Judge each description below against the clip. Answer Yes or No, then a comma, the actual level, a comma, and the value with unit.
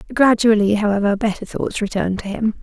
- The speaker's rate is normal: Yes, average, 160 wpm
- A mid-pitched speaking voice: No, high, 210 Hz